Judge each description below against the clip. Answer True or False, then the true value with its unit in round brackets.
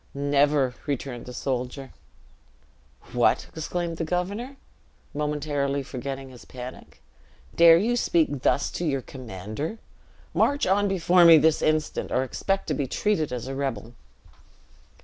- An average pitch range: True (4.3 semitones)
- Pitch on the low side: False (145 Hz)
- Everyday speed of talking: False (130 wpm)